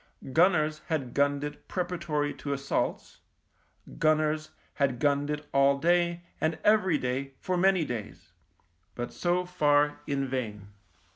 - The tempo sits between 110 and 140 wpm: Yes, slow, 135 wpm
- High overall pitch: No, medium, 150 Hz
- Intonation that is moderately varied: Yes, average, 3.7 semitones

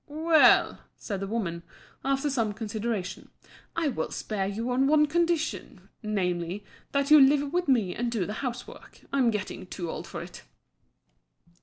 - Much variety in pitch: Yes, wide, 6.1 semitones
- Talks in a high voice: Yes, high, 230 Hz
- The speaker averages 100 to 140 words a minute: No, average, 155 wpm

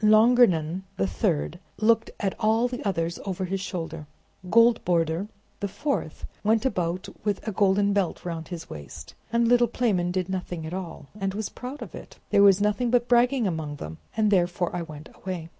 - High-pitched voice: Yes, high, 195 Hz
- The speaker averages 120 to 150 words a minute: No, average, 180 wpm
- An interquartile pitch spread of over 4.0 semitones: Yes, average, 4.5 semitones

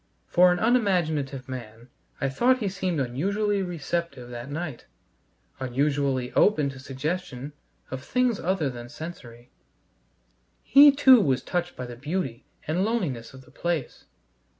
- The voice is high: No, medium, 150 Hz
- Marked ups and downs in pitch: Yes, wide, 6.4 semitones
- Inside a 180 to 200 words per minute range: No, slow, 135 wpm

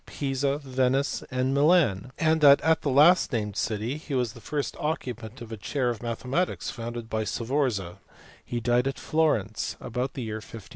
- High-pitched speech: No, low, 125 Hz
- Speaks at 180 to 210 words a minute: Yes, average, 185 wpm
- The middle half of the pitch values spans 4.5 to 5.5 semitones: No, average, 3.9 semitones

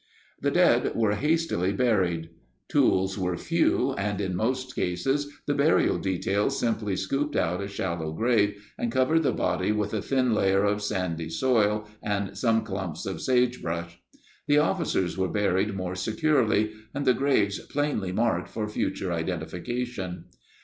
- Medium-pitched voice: No, low, 105 Hz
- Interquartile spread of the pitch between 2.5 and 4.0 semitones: No, average, 5.2 semitones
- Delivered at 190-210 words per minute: No, average, 150 wpm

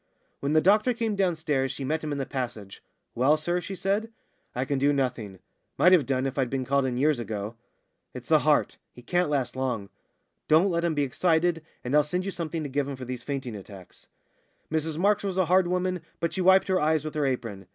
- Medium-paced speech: No, fast, 225 wpm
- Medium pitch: Yes, medium, 150 Hz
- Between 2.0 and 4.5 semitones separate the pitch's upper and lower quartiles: No, wide, 5.4 semitones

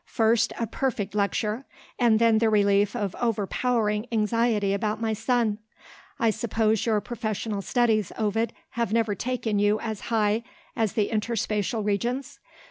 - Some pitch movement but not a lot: No, narrow, 1.9 semitones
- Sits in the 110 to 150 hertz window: No, high, 220 Hz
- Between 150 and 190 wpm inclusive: No, average, 140 wpm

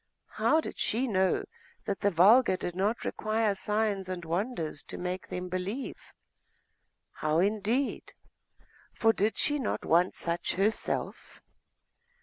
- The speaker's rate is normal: No, slow, 130 wpm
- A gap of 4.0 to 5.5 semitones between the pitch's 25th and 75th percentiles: No, average, 3.6 semitones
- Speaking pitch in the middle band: No, high, 200 Hz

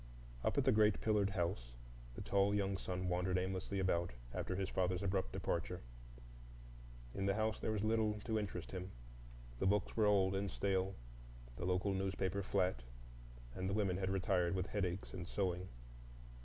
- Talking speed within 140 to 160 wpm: No, average, 170 wpm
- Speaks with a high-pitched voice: No, very low, 95 Hz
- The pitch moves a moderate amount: No, narrow, 1.6 semitones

